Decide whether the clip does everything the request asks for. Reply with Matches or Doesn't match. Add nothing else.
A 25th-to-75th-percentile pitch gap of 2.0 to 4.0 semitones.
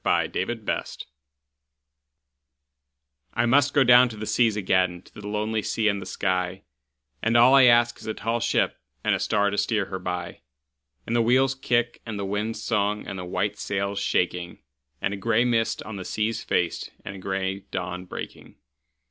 Matches